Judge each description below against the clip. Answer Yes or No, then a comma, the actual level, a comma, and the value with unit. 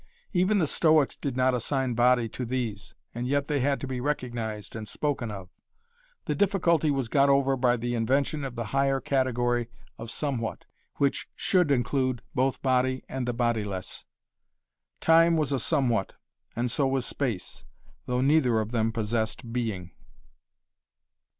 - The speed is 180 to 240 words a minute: No, average, 155 wpm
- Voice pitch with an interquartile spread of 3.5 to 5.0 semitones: No, average, 3.1 semitones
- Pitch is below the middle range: Yes, low, 125 Hz